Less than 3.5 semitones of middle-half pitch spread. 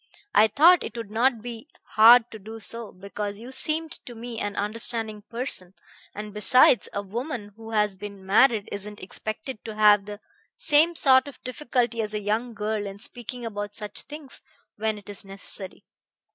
Yes: average, 2.9 semitones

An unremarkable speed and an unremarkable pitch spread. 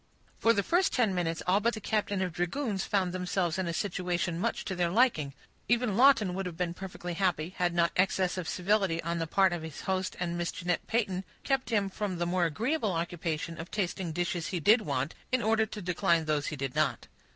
No: fast, 220 wpm; average, 3.2 semitones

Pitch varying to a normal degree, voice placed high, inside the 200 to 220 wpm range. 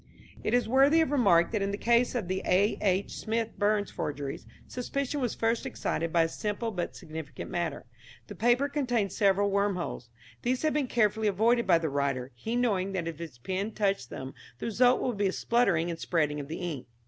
No: wide, 5.9 semitones; high, 200 Hz; fast, 205 wpm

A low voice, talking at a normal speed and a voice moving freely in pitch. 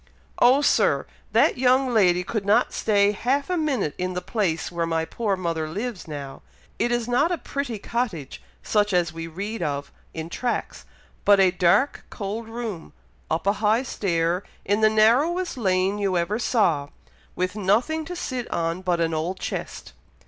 No: high, 200 Hz; average, 170 wpm; wide, 5.8 semitones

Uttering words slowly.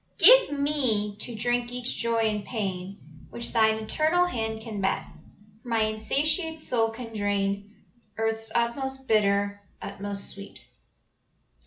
Yes: slow, 130 wpm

